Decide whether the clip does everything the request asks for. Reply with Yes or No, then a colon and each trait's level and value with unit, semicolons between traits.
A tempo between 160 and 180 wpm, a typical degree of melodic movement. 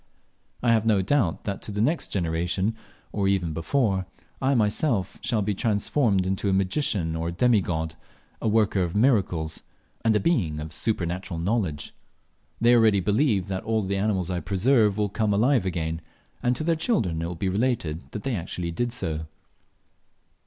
Yes: average, 175 wpm; average, 4.6 semitones